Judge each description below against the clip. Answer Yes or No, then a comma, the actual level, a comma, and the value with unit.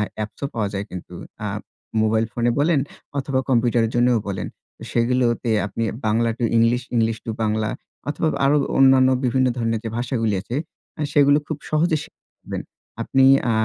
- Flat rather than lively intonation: No, average, 3.0 semitones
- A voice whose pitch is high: No, low, 120 Hz